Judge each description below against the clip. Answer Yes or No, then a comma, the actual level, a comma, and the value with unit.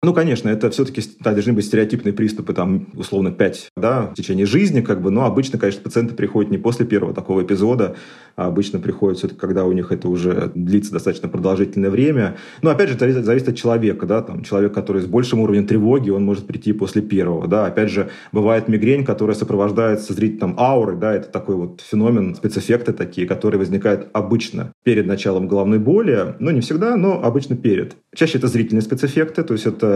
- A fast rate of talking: Yes, fast, 195 wpm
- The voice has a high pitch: No, low, 110 Hz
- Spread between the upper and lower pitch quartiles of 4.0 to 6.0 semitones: No, average, 3.3 semitones